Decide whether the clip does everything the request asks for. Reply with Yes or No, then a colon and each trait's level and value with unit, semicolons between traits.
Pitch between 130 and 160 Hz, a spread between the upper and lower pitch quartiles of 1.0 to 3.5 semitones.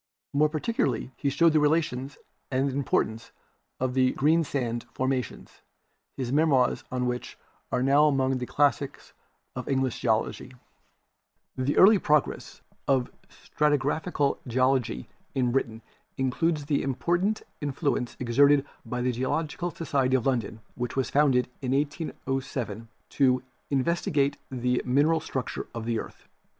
Yes: low, 135 Hz; average, 2.7 semitones